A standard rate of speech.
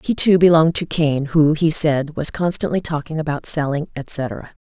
Yes: average, 180 wpm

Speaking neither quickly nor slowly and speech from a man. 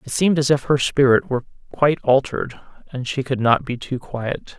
No: fast, 210 wpm; male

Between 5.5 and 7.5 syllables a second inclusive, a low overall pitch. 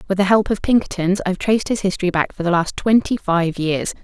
No: 6.2 syllables/s; high, 190 Hz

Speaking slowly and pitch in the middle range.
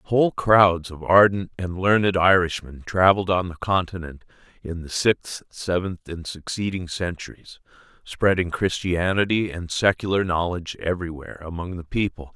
No: slow, 130 wpm; very low, 90 Hz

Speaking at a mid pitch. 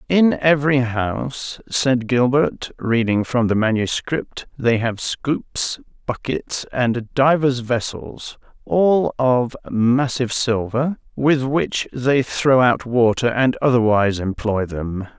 No: low, 125 Hz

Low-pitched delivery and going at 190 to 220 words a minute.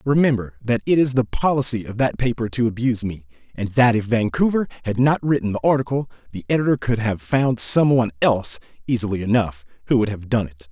Yes: low, 115 Hz; average, 200 wpm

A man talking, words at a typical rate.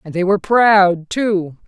No: female; average, 180 wpm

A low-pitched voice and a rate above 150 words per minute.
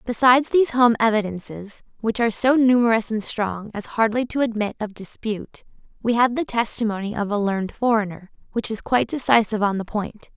No: high, 225 Hz; average, 180 wpm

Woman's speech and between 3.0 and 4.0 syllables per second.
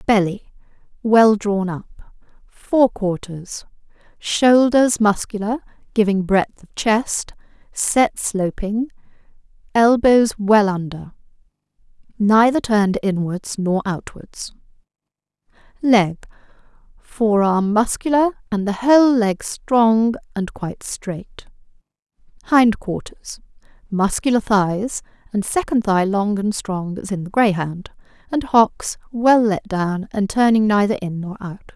Yes: female; 3.7 syllables/s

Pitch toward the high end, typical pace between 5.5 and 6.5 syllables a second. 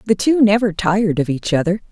Yes: high, 195 Hz; 6.0 syllables/s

